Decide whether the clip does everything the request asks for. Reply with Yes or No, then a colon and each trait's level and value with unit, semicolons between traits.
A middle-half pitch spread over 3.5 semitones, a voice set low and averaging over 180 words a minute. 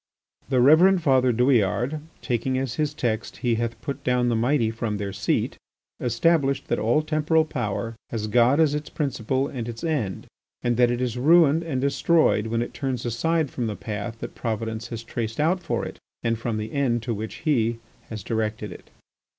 Yes: average, 4.1 semitones; low, 120 Hz; average, 190 wpm